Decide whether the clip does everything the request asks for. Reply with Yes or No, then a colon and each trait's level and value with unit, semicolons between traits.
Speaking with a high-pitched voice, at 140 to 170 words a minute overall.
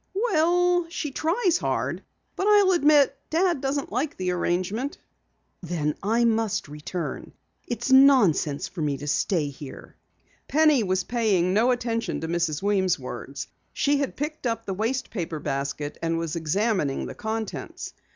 Yes: high, 220 Hz; average, 150 wpm